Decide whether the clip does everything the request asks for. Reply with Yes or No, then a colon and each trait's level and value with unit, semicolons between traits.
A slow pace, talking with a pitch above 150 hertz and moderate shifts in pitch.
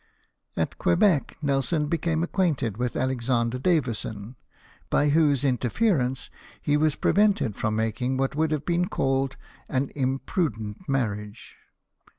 No: slow, 120 wpm; low, 135 Hz; average, 4.6 semitones